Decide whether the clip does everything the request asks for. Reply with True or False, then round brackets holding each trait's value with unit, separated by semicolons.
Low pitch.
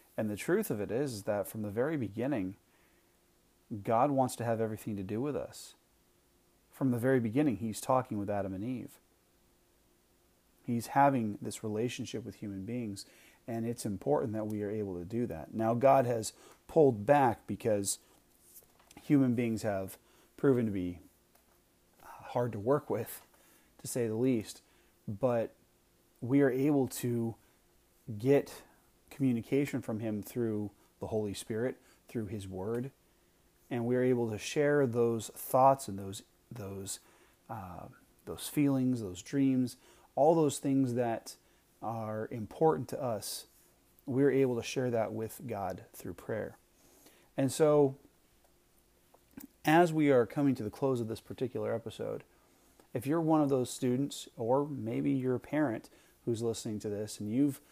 True (115 Hz)